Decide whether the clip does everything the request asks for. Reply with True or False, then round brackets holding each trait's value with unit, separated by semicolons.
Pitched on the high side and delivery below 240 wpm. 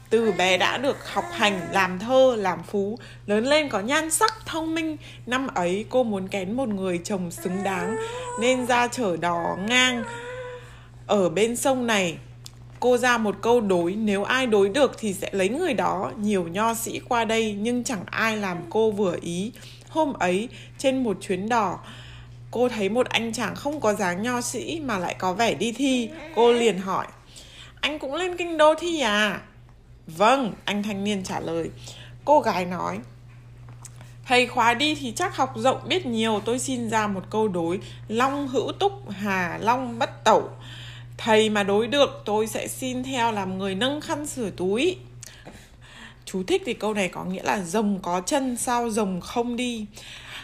True (215 Hz; 185 wpm)